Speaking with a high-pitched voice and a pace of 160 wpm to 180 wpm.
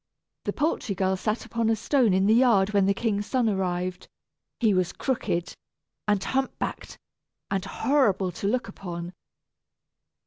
No: high, 200 Hz; average, 150 wpm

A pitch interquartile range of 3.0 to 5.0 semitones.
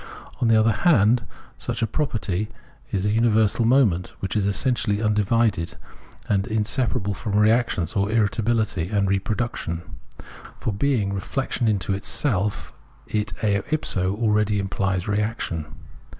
No: narrow, 2.6 semitones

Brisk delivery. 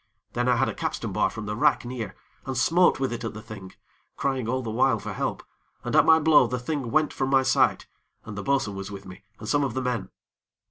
Yes: fast, 245 wpm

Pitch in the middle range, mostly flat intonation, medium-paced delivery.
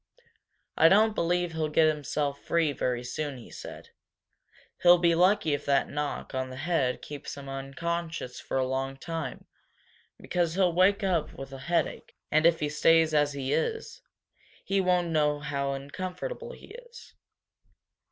No: medium, 155 Hz; average, 4.1 semitones; average, 160 wpm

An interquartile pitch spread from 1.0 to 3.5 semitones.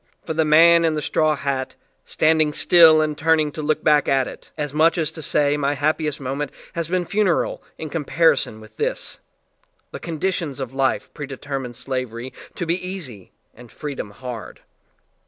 Yes: average, 3.1 semitones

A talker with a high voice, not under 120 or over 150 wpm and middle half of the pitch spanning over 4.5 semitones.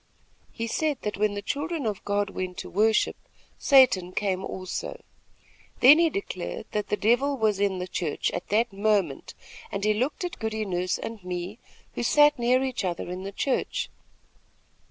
No: high, 210 Hz; average, 175 wpm; average, 5.1 semitones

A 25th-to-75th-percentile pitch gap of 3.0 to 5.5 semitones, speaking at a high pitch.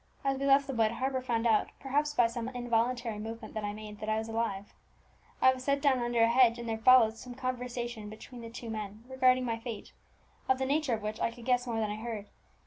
No: narrow, 2.4 semitones; high, 235 Hz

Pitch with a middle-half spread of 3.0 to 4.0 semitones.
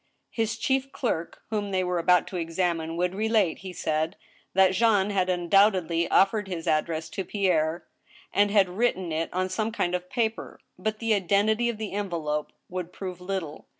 Yes: average, 3.6 semitones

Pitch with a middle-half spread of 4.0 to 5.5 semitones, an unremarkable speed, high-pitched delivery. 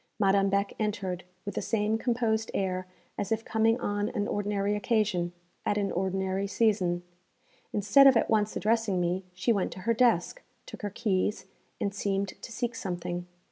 No: narrow, 2.6 semitones; average, 170 wpm; high, 205 Hz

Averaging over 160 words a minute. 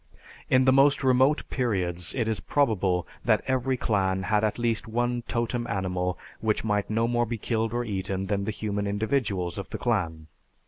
Yes: average, 180 wpm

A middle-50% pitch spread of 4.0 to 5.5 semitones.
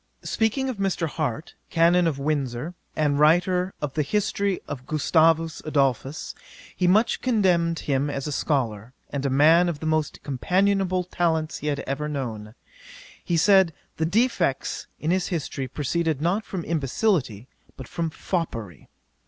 Yes: average, 4.4 semitones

